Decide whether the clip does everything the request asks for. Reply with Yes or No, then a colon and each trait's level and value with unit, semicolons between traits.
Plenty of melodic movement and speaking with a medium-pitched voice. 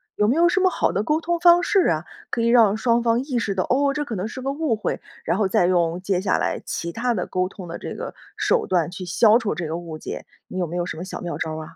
No: wide, 6.5 semitones; high, 210 Hz